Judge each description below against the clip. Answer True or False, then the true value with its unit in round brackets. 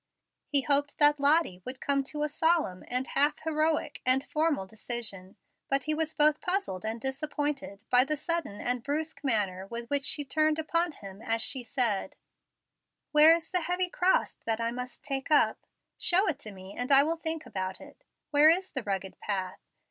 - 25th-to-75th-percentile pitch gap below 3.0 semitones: False (5.3 semitones)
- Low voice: False (280 Hz)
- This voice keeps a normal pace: True (185 wpm)